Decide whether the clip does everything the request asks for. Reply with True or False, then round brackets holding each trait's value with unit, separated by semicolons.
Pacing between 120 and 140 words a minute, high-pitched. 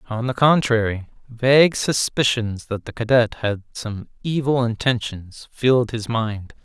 False (135 wpm; 115 Hz)